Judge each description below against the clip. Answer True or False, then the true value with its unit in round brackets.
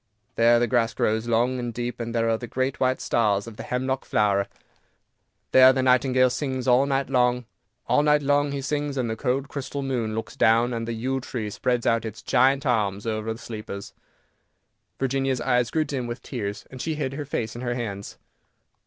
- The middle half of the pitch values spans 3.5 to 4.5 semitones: False (2.7 semitones)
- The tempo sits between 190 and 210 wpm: True (195 wpm)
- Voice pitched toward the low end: True (125 Hz)